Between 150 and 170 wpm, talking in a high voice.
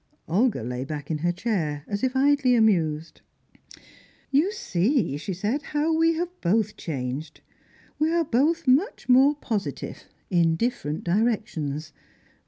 No: slow, 135 wpm; high, 215 Hz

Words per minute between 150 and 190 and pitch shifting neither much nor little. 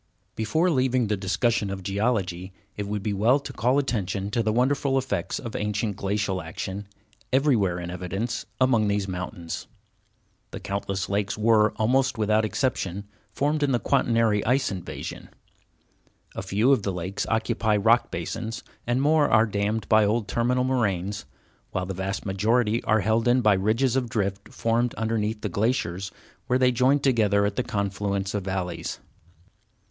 Yes: average, 160 wpm; average, 3.6 semitones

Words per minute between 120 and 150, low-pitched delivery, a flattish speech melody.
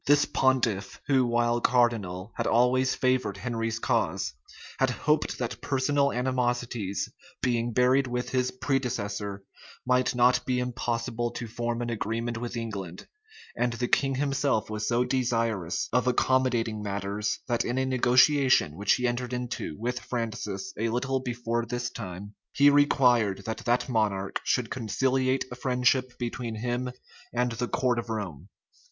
Yes: average, 145 wpm; low, 120 Hz; narrow, 2.2 semitones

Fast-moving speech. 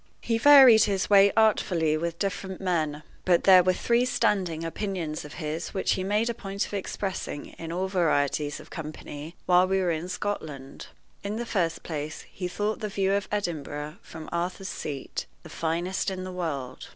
No: average, 180 wpm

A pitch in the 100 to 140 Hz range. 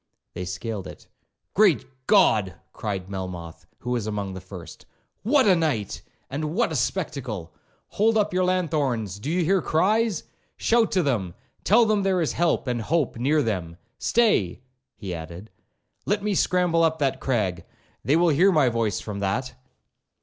Yes: low, 135 Hz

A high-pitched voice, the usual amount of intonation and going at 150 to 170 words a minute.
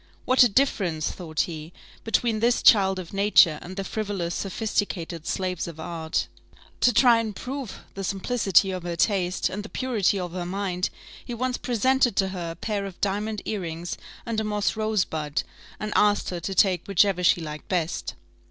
No: high, 195 Hz; average, 3.7 semitones; average, 180 wpm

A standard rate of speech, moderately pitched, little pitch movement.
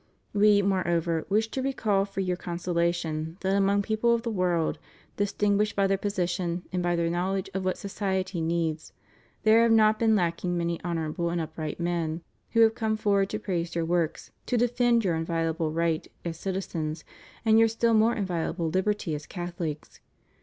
No: average, 175 wpm; medium, 180 Hz; average, 3.6 semitones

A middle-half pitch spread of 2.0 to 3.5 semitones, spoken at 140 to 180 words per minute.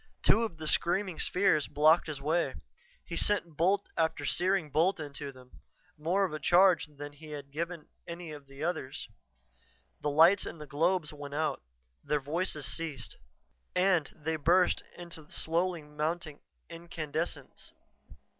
Yes: average, 2.8 semitones; average, 145 wpm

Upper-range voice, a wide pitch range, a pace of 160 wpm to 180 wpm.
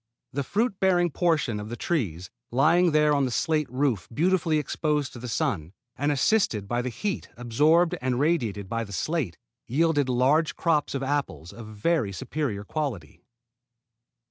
No: medium, 140 Hz; wide, 5.9 semitones; average, 165 wpm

